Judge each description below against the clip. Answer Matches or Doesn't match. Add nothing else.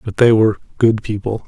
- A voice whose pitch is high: Doesn't match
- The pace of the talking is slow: Doesn't match